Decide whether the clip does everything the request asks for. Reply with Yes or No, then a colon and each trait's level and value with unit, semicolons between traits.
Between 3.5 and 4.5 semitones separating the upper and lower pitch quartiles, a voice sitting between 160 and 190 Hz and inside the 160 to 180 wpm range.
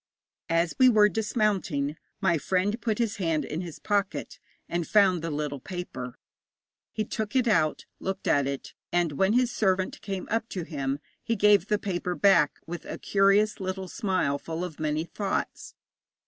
Yes: average, 4.2 semitones; medium, 185 Hz; average, 170 wpm